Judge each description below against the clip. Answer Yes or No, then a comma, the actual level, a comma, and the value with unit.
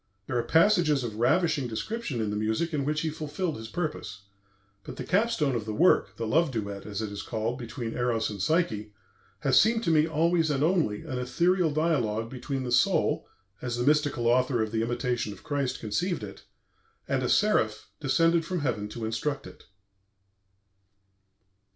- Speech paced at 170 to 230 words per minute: Yes, average, 180 wpm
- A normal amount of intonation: No, wide, 6.3 semitones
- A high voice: No, low, 130 Hz